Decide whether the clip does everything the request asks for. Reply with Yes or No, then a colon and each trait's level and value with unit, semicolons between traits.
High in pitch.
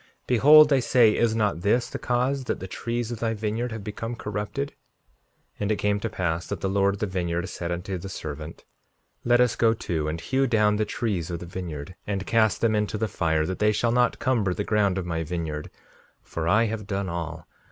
No: low, 105 Hz